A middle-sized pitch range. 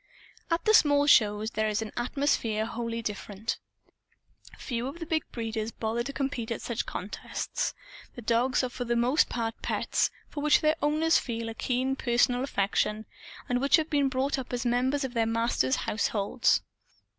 Yes: average, 3.5 semitones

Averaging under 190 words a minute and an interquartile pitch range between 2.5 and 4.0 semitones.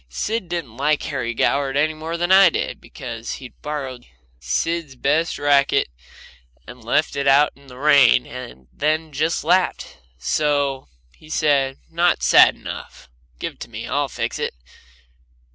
Yes: average, 155 wpm; average, 3.1 semitones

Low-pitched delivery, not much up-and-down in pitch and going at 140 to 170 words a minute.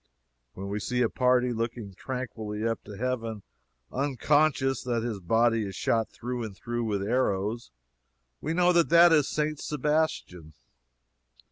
No: low, 120 Hz; average, 3.8 semitones; average, 145 wpm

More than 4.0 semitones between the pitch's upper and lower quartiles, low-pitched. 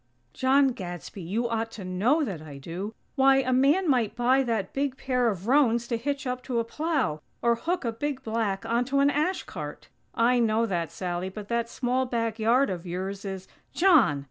No: average, 5.1 semitones; high, 235 Hz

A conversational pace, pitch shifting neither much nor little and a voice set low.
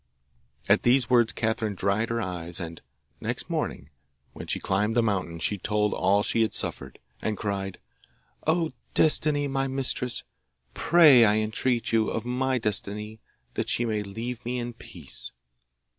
Yes: average, 155 wpm; average, 3.4 semitones; low, 110 Hz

